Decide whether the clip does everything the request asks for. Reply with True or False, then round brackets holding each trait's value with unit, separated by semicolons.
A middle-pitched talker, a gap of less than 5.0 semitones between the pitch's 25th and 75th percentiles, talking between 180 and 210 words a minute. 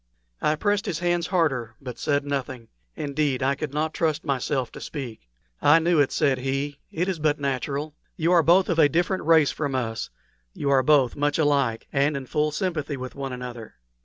True (145 Hz; 3.1 semitones; 195 wpm)